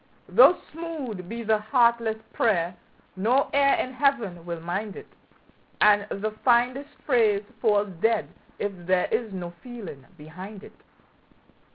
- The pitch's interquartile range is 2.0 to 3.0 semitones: No, average, 4.4 semitones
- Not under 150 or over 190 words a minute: No, slow, 135 wpm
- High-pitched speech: Yes, high, 220 Hz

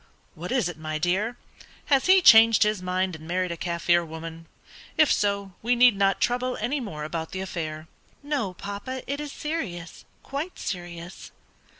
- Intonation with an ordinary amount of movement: No, wide, 6.3 semitones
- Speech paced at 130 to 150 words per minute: No, average, 170 wpm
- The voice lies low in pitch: No, high, 190 Hz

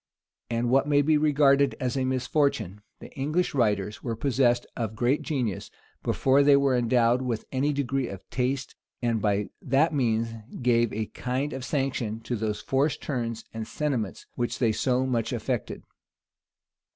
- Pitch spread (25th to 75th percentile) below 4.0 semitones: Yes, average, 3.2 semitones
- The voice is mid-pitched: No, low, 125 Hz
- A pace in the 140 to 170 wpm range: Yes, average, 160 wpm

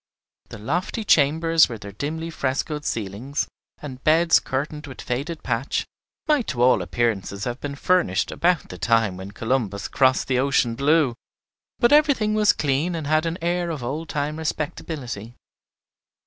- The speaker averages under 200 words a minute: Yes, average, 155 wpm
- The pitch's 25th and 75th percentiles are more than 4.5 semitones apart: Yes, wide, 5.4 semitones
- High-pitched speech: No, medium, 140 Hz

